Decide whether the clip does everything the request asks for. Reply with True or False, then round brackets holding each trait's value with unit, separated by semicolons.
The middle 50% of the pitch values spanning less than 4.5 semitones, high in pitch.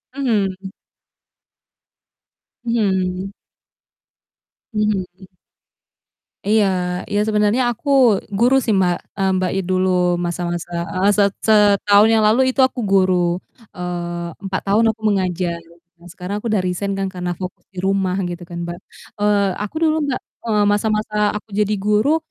True (2.6 semitones; 200 Hz)